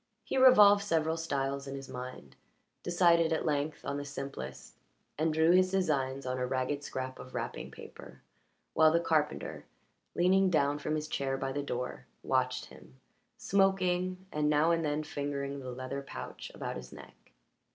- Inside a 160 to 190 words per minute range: Yes, average, 165 wpm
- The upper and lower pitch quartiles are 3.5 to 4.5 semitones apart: Yes, average, 3.9 semitones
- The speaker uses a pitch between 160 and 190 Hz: No, medium, 145 Hz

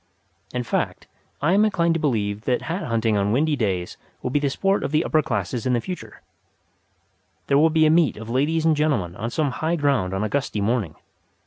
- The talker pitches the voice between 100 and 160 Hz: Yes, low, 135 Hz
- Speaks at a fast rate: Yes, fast, 215 wpm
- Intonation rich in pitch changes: Yes, wide, 6.3 semitones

